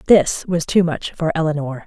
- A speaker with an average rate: Yes, average, 195 wpm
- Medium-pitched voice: Yes, medium, 160 Hz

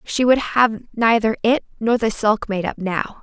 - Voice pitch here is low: No, high, 225 Hz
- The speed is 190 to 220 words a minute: Yes, fast, 205 wpm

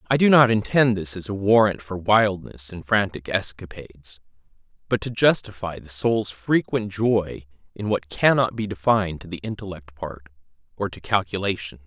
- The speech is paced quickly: No, average, 155 wpm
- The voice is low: Yes, low, 100 Hz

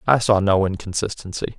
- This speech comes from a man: Yes, male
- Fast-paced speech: No, average, 150 wpm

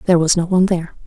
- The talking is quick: Yes, fast, 280 wpm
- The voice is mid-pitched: Yes, medium, 175 Hz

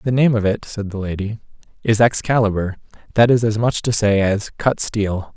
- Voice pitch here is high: No, low, 110 Hz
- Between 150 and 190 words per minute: No, average, 200 wpm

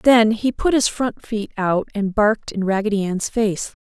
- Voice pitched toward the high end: Yes, high, 215 Hz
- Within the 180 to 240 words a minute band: Yes, fast, 205 wpm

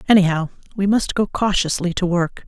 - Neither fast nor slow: Yes, average, 170 wpm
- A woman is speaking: Yes, female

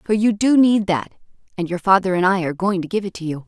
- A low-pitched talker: No, high, 190 Hz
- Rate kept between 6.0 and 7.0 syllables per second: Yes, 6.2 syllables/s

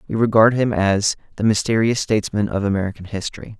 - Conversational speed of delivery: Yes, average, 165 wpm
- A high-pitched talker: No, low, 105 Hz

